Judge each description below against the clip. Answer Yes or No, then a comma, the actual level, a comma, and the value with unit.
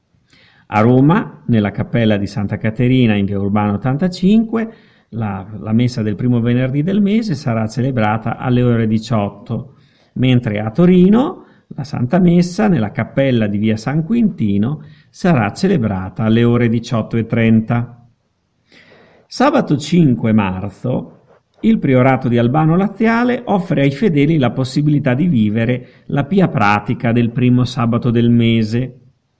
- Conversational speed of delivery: Yes, average, 130 wpm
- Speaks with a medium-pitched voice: No, low, 125 Hz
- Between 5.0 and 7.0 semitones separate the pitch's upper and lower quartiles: Yes, wide, 5.6 semitones